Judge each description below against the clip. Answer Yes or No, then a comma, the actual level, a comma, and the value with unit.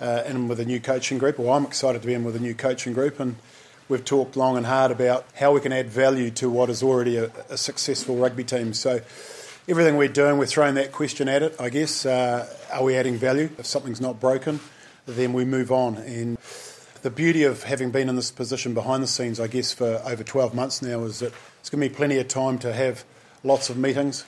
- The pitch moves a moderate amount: No, narrow, 1.9 semitones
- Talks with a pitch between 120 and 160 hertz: Yes, low, 130 Hz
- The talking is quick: Yes, fast, 255 wpm